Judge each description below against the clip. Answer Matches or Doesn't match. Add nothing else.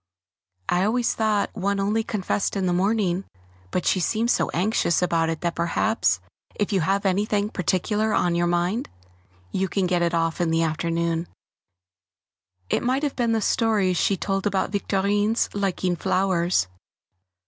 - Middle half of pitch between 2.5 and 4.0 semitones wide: Matches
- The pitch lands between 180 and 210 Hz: Matches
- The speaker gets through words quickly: Doesn't match